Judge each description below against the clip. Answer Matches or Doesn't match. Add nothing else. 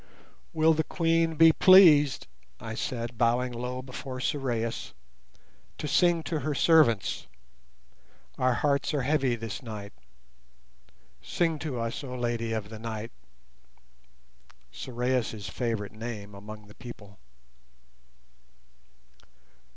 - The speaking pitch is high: Doesn't match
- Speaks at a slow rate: Matches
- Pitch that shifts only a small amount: Doesn't match